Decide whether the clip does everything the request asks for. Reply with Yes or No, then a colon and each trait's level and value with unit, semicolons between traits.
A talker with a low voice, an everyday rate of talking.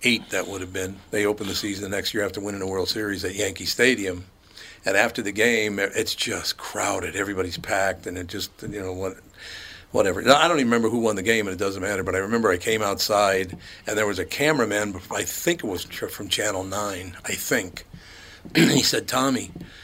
No: low, 100 Hz; fast, 215 wpm